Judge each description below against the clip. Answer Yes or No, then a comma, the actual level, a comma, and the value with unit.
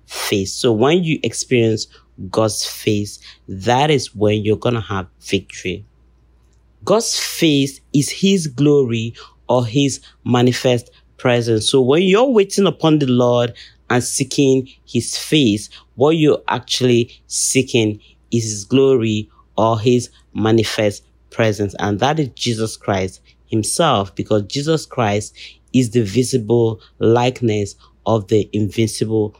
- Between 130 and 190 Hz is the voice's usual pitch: No, low, 115 Hz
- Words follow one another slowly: Yes, slow, 125 wpm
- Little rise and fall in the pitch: No, average, 3.8 semitones